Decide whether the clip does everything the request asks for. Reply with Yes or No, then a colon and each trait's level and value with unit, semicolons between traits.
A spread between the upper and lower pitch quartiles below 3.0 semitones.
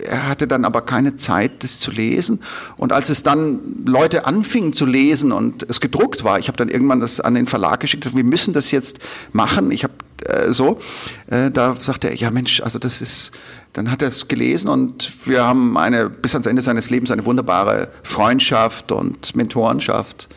Yes: narrow, 2.4 semitones